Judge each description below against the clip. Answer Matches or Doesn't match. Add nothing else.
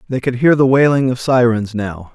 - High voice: Doesn't match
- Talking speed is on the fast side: Matches